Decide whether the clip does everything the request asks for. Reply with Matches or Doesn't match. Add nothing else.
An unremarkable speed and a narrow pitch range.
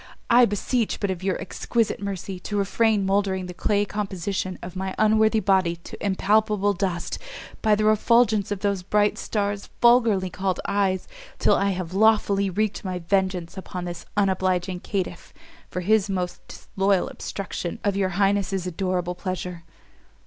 Matches